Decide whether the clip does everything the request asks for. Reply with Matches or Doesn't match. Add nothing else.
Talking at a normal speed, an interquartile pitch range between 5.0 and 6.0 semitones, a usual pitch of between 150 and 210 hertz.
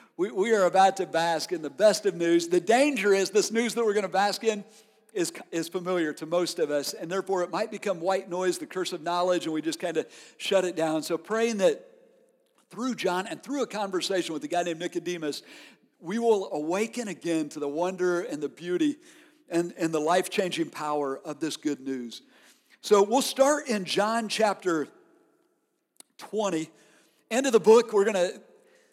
Matches